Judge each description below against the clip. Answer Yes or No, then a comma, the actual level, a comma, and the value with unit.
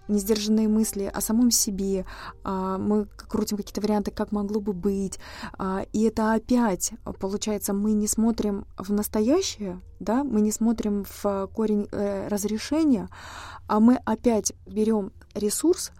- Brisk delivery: No, average, 130 wpm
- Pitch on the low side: No, high, 210 Hz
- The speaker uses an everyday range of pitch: No, narrow, 1.5 semitones